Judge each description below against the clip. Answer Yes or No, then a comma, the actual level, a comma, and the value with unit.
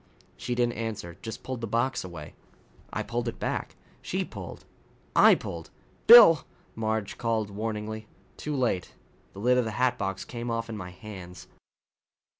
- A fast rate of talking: No, average, 160 wpm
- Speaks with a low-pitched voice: Yes, low, 115 Hz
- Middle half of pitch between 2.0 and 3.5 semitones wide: Yes, average, 3.0 semitones